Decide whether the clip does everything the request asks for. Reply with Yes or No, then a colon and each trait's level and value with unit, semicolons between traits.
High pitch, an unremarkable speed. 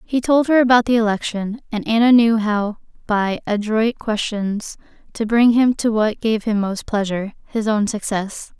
Yes: high, 220 Hz; average, 170 wpm